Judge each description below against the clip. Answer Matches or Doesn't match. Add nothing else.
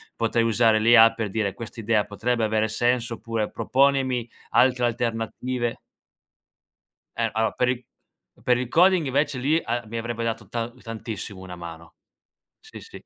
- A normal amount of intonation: Doesn't match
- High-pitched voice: Doesn't match